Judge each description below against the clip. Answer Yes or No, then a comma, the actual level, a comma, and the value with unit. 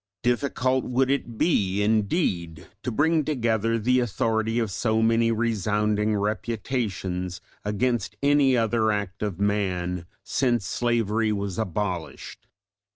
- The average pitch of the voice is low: Yes, low, 110 Hz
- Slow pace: Yes, slow, 115 wpm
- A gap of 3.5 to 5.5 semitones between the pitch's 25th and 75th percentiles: No, average, 2.9 semitones